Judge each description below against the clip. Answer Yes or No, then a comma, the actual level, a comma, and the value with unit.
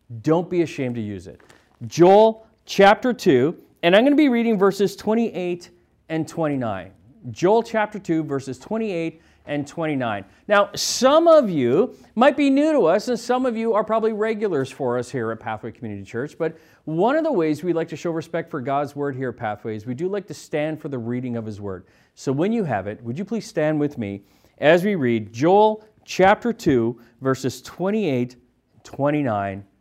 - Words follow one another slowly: No, average, 195 wpm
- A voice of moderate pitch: Yes, medium, 155 Hz